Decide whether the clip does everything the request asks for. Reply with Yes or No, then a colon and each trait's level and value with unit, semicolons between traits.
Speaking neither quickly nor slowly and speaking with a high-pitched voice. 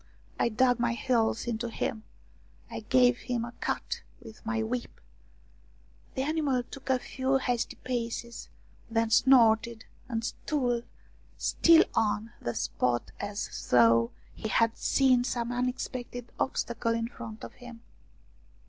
No: slow, 130 wpm; high, 235 Hz